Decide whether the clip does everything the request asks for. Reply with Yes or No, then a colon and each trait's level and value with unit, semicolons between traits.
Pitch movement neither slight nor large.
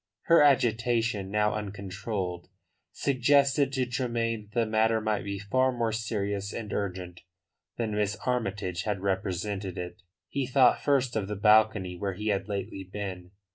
Yes: average, 3.2 semitones